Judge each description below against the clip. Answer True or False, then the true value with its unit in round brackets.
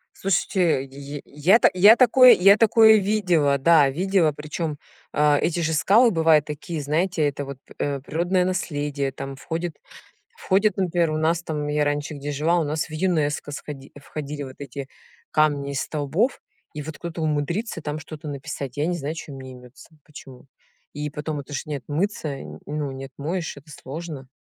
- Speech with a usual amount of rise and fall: True (3.3 semitones)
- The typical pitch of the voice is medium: True (150 Hz)